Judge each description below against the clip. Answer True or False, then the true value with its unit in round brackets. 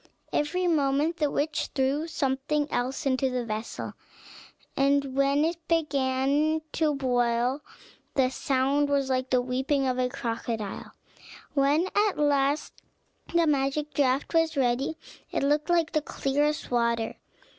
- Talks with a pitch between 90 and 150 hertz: False (275 Hz)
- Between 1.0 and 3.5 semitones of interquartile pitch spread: True (2.6 semitones)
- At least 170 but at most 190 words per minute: False (135 wpm)